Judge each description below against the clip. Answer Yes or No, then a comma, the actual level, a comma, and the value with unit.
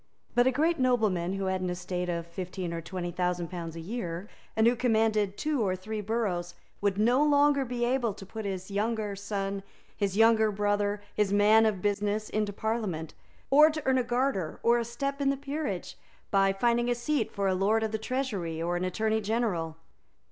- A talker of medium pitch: No, high, 210 Hz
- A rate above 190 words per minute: Yes, average, 200 wpm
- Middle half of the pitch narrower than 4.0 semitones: No, average, 4.3 semitones